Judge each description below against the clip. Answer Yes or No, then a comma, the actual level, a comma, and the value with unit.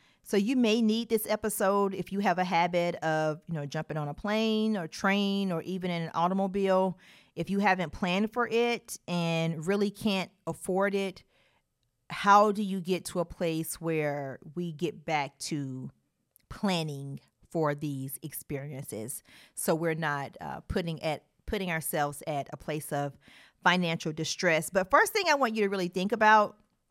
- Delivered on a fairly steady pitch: No, average, 4.3 semitones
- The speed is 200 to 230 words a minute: No, average, 170 wpm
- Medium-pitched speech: Yes, medium, 175 Hz